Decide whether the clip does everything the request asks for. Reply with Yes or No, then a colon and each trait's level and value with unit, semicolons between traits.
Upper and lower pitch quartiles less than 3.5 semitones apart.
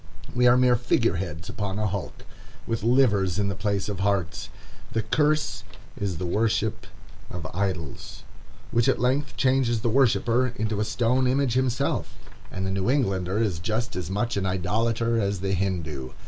No: average, 4.3 semitones